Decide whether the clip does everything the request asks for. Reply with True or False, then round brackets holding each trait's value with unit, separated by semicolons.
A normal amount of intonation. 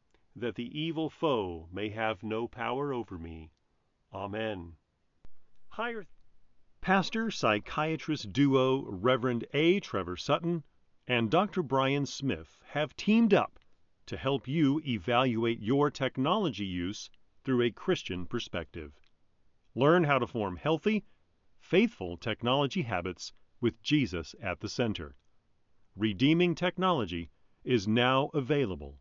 False (7.1 semitones)